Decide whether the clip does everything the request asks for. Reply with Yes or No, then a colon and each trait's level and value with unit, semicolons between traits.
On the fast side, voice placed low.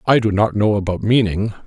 Yes: fast, 215 wpm; low, 105 Hz